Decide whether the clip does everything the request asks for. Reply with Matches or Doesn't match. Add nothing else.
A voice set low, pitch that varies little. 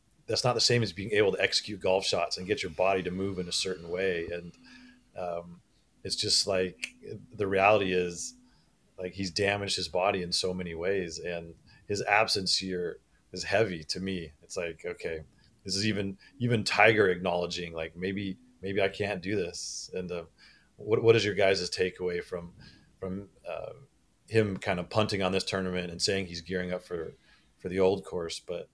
Matches